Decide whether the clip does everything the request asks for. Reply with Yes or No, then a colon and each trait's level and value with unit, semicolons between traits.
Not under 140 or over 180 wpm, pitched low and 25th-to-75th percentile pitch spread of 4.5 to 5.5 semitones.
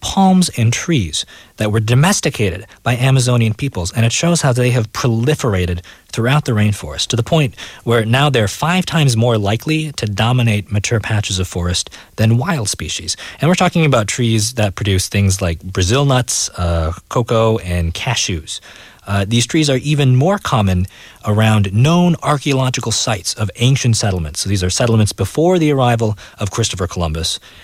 Yes: average, 170 wpm; low, 115 Hz; average, 5.1 semitones